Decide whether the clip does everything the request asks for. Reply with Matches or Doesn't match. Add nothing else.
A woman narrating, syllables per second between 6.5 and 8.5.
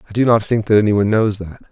Doesn't match